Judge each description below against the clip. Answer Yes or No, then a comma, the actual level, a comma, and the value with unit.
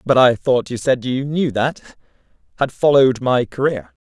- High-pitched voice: No, low, 125 Hz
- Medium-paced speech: Yes, average, 165 wpm